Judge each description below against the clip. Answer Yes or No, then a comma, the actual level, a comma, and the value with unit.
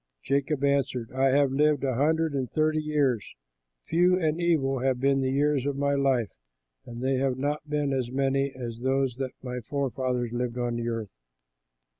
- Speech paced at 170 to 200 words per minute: Yes, average, 175 wpm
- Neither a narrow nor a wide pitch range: No, narrow, 2.3 semitones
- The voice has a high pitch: No, low, 135 Hz